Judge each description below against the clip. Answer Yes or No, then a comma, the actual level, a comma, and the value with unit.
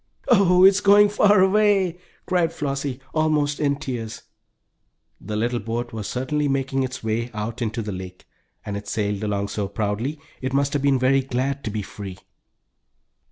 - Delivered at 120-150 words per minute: No, average, 165 wpm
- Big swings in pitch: Yes, wide, 5.7 semitones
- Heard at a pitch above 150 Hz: No, low, 130 Hz